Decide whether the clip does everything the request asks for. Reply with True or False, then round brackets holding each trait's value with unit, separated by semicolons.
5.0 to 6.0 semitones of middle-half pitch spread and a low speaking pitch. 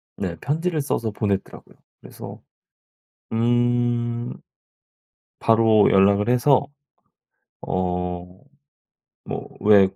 False (3.8 semitones; 115 Hz)